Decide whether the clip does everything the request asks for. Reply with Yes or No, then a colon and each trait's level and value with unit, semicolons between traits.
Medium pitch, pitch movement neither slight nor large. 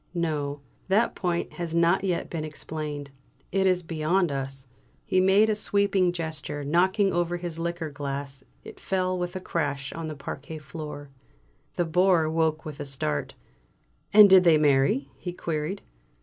Yes: medium, 165 Hz; average, 3.8 semitones